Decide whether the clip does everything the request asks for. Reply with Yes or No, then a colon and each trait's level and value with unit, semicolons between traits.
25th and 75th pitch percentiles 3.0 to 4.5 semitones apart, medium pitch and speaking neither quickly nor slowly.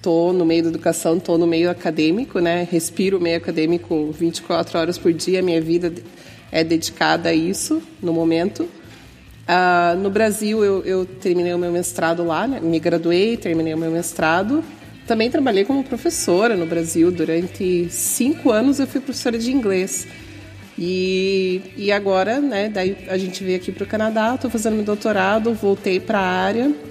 Yes: average, 3.7 semitones; medium, 180 Hz; average, 170 wpm